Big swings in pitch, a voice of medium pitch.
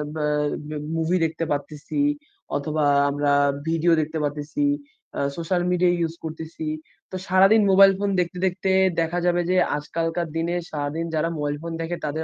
No: narrow, 2.5 semitones; medium, 165 Hz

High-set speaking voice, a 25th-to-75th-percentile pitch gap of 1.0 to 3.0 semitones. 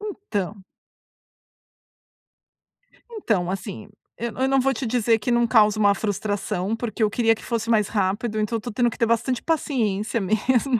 Yes: high, 225 Hz; narrow, 2.6 semitones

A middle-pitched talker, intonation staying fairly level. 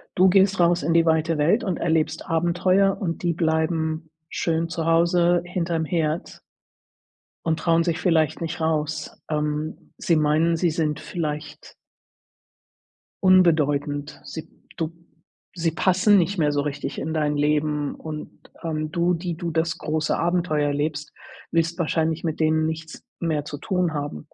Yes: medium, 160 Hz; narrow, 1.9 semitones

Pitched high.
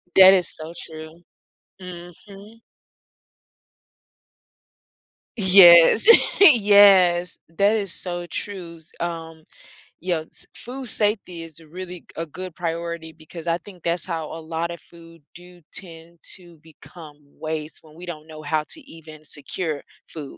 No: medium, 170 Hz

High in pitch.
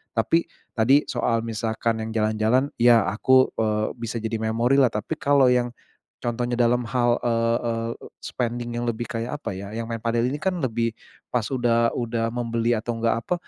No: low, 115 Hz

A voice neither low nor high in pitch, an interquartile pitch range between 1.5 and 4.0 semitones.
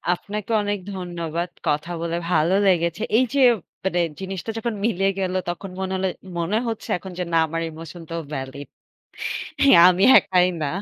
Yes: medium, 180 Hz; average, 2.7 semitones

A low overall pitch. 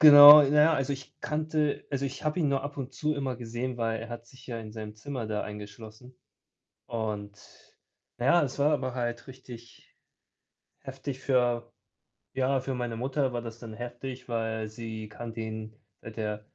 Yes: low, 120 Hz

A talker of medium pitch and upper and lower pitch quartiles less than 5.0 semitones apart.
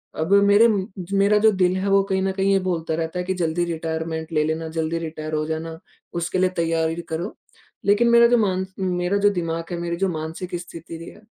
Yes: medium, 175 Hz; average, 3.1 semitones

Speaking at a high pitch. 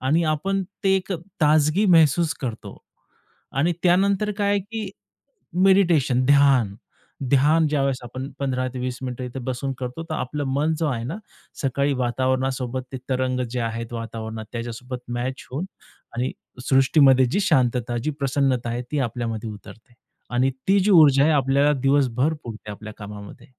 No: low, 130 Hz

